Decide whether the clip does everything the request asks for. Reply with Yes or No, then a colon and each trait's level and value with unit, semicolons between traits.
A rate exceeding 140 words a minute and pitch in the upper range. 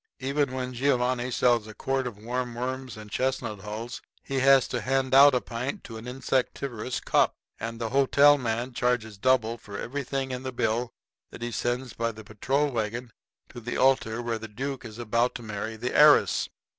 No: average, 190 wpm; low, 125 Hz